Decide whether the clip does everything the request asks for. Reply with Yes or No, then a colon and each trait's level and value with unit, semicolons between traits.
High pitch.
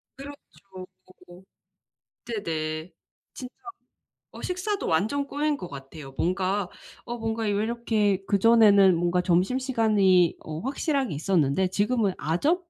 Yes: high, 205 Hz